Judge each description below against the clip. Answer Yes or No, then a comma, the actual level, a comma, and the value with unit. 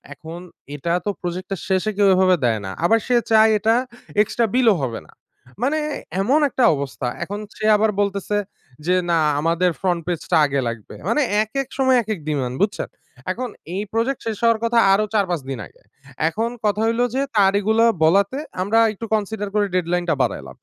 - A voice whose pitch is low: No, high, 200 Hz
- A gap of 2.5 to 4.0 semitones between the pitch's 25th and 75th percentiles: No, average, 4.5 semitones